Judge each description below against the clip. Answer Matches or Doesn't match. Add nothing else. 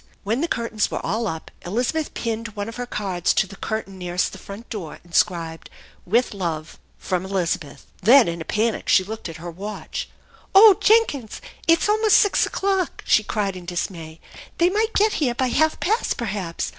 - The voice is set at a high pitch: Matches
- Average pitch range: Doesn't match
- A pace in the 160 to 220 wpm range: Matches